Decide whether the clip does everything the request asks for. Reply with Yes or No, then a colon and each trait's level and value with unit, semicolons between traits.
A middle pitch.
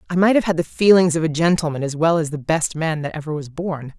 Yes: medium, 160 Hz